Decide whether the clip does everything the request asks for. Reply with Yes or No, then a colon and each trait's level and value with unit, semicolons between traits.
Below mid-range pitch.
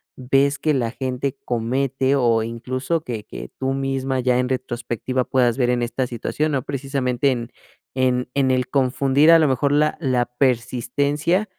Yes: low, 130 Hz